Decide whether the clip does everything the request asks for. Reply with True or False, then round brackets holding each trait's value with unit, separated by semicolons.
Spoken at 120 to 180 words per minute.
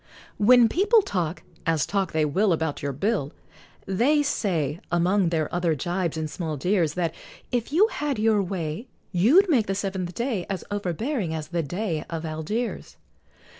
True (165 wpm)